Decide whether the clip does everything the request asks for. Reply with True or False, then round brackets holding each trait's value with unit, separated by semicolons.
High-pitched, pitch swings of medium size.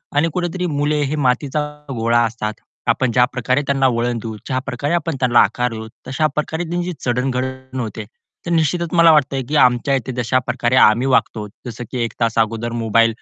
False (130 Hz; 3.9 semitones)